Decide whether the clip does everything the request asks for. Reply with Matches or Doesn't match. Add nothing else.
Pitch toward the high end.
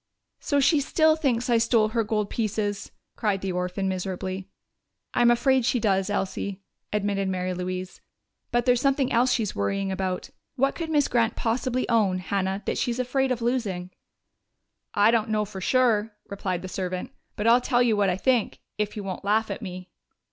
Matches